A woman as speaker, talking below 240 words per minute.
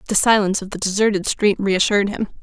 Yes: female; average, 200 wpm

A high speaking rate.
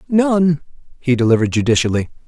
No: slow, 105 wpm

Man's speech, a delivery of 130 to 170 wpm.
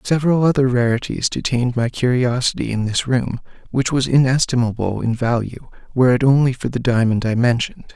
Yes: male; average, 165 wpm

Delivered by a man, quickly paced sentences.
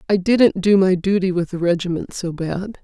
No: female; fast, 210 wpm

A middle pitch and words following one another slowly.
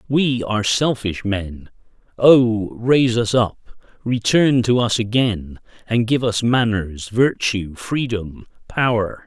No: low, 115 Hz; slow, 125 wpm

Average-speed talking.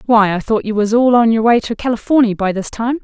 No: fast, 275 wpm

